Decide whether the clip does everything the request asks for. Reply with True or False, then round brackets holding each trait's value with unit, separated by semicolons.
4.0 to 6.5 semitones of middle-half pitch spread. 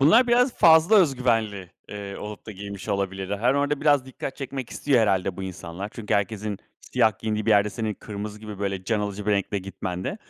True (4.5 semitones)